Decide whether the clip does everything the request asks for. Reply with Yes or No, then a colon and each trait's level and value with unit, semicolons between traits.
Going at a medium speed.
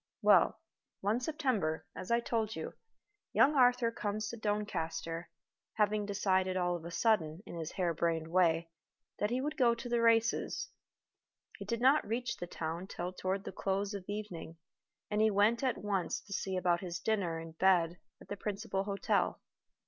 Yes: average, 175 wpm